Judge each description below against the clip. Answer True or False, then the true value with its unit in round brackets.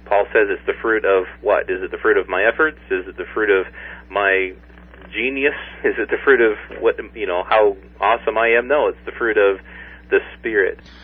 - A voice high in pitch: True (395 Hz)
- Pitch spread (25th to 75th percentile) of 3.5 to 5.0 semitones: True (3.8 semitones)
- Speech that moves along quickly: True (220 wpm)